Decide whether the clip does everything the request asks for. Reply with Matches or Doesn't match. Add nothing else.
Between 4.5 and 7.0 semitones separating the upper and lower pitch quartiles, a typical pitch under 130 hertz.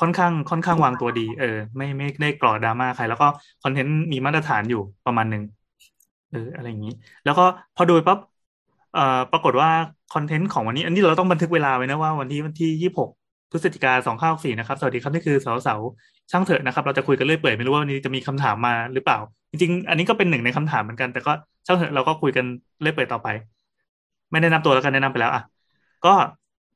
Doesn't match